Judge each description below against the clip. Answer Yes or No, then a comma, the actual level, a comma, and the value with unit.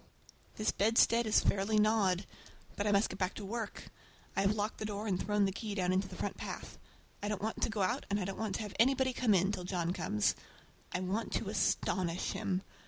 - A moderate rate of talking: No, fast, 225 wpm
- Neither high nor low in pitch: No, high, 200 Hz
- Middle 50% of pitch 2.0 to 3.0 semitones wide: Yes, narrow, 2.5 semitones